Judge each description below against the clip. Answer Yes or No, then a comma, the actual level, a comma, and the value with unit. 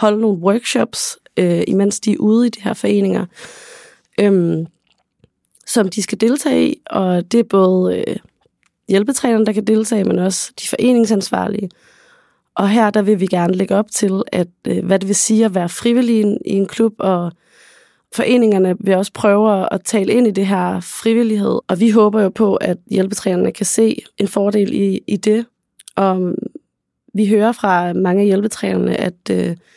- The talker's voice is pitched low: No, high, 205 Hz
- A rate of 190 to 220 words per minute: No, average, 175 wpm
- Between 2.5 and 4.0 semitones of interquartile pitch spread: Yes, average, 2.8 semitones